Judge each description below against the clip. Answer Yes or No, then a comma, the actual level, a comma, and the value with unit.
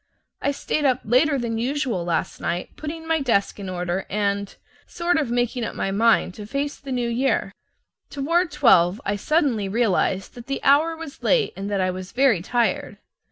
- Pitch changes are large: Yes, wide, 6.2 semitones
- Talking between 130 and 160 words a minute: No, average, 185 wpm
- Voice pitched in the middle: No, high, 240 Hz